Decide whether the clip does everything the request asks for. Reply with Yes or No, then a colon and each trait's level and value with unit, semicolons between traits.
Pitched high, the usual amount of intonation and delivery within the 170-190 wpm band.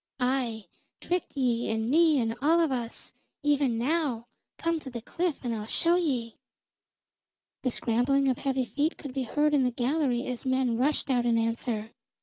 Yes: very high, 255 Hz; average, 3.9 semitones; average, 175 wpm